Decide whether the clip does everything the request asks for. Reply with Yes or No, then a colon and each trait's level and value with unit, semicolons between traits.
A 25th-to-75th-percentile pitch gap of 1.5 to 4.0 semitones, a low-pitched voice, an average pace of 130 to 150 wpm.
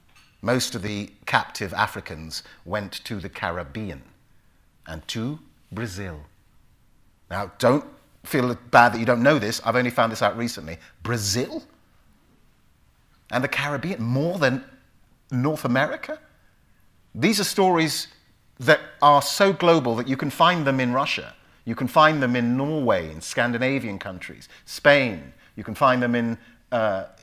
No: average, 5.2 semitones; low, 120 Hz; average, 145 wpm